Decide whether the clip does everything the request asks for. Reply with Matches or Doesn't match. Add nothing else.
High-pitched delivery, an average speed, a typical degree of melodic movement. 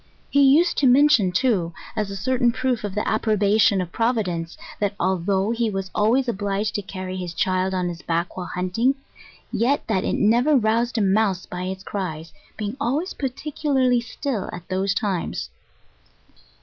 Matches